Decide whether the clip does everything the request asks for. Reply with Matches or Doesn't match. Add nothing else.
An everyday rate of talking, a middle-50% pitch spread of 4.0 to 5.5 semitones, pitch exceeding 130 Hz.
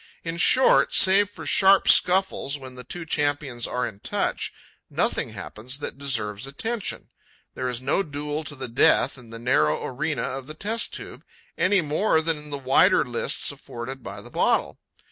Matches